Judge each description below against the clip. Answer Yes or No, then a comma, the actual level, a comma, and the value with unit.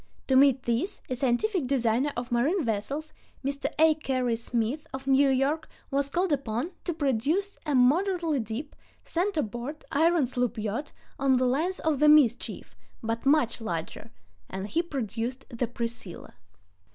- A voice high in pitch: Yes, very high, 270 Hz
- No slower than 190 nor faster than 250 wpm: No, average, 150 wpm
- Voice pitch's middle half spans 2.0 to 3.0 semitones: No, average, 4.4 semitones